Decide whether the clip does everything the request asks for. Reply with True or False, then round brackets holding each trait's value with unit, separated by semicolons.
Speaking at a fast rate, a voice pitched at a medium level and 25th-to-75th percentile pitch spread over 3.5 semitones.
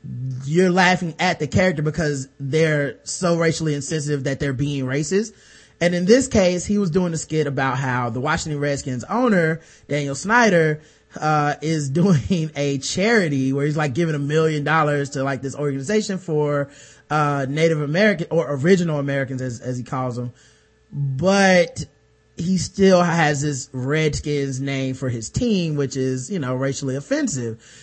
False (160 wpm; 150 Hz; 3.9 semitones)